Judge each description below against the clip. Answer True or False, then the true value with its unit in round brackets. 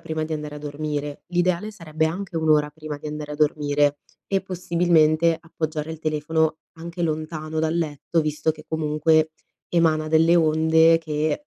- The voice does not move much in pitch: True (1.4 semitones)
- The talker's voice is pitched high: False (155 Hz)